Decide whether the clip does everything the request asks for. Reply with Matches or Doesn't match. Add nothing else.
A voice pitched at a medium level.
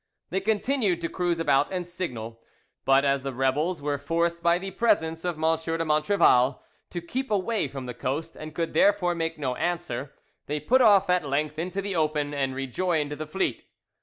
Matches